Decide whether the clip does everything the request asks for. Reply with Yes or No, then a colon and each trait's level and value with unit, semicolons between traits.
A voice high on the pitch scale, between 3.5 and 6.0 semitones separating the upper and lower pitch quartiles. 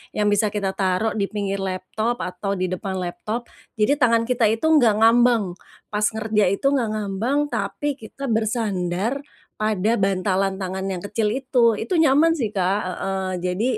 No: high, 210 Hz; average, 3.1 semitones